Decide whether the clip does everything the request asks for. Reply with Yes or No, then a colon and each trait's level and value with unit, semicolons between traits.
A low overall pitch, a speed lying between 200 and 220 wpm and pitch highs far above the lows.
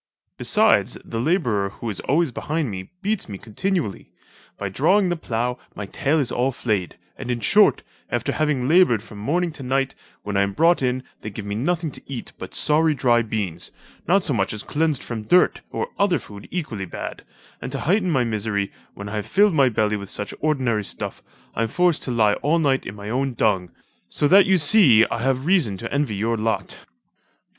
Yes: low, 125 Hz; fast, 205 wpm; wide, 7.0 semitones